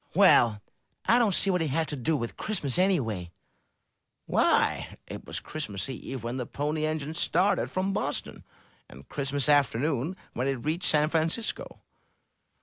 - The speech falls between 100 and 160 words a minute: Yes, average, 150 wpm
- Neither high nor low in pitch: Yes, medium, 150 Hz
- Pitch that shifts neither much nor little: Yes, average, 4.3 semitones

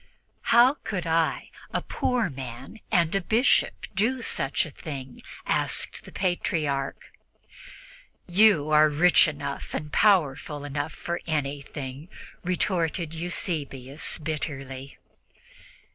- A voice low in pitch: No, medium, 155 Hz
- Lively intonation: No, average, 4.3 semitones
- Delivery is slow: Yes, slow, 105 wpm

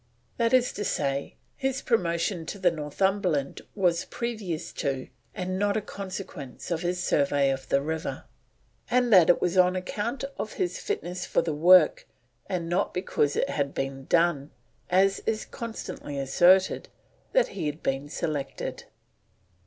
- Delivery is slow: No, average, 155 wpm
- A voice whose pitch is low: No, medium, 175 Hz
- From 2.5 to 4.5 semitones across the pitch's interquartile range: No, average, 4.9 semitones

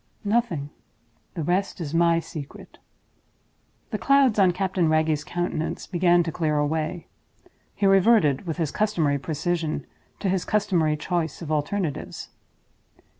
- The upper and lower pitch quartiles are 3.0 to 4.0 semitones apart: Yes, average, 3.6 semitones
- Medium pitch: Yes, medium, 170 Hz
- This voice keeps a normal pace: No, slow, 130 wpm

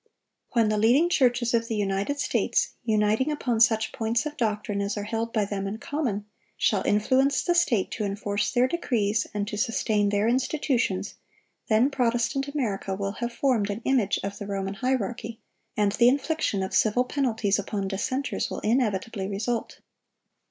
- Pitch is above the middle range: Yes, high, 225 Hz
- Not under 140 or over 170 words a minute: Yes, average, 165 wpm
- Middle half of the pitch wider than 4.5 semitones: No, average, 3.7 semitones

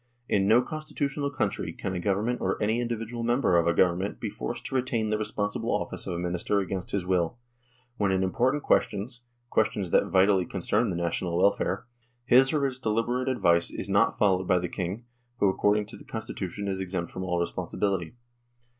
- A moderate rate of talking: Yes, average, 190 wpm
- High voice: No, low, 100 Hz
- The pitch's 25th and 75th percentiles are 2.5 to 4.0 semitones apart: No, average, 4.4 semitones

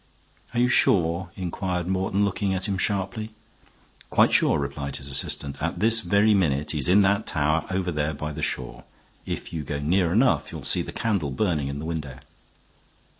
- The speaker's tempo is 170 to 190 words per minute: Yes, average, 185 wpm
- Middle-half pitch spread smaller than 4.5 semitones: No, average, 5.0 semitones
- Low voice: Yes, very low, 90 Hz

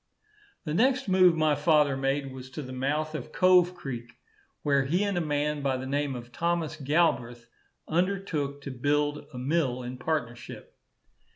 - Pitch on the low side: No, medium, 145 Hz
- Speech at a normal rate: Yes, average, 165 wpm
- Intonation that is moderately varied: Yes, average, 3.8 semitones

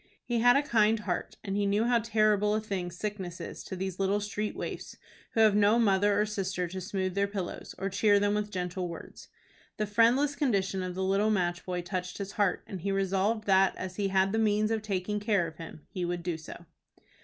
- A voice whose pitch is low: No, high, 200 Hz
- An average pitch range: No, narrow, 2.3 semitones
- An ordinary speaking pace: No, fast, 225 wpm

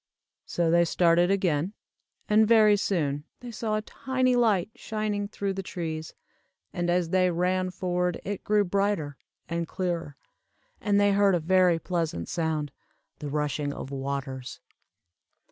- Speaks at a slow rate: No, average, 145 wpm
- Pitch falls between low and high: Yes, medium, 180 Hz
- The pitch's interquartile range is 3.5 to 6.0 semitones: Yes, average, 4.1 semitones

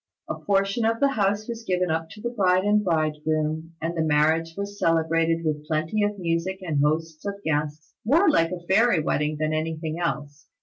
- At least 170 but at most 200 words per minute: Yes, average, 190 wpm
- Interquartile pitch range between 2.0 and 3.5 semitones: No, average, 4.3 semitones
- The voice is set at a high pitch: No, medium, 165 Hz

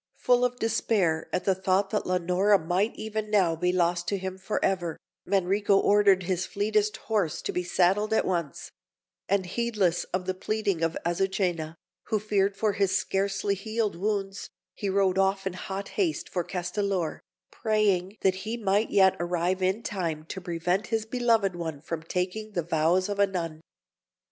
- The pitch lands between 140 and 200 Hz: Yes, high, 190 Hz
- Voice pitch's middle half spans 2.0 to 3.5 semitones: Yes, average, 2.7 semitones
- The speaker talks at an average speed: Yes, average, 170 wpm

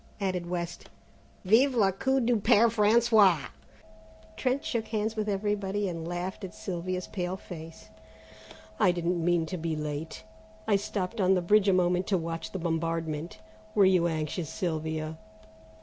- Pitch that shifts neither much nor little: Yes, average, 3.8 semitones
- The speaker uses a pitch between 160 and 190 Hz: Yes, medium, 185 Hz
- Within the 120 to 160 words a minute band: Yes, average, 150 wpm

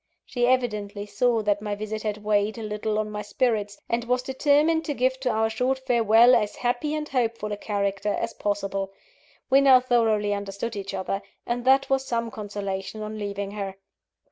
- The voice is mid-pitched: No, high, 220 Hz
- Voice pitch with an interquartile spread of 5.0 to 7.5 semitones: No, average, 3.3 semitones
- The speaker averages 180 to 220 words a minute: Yes, average, 185 wpm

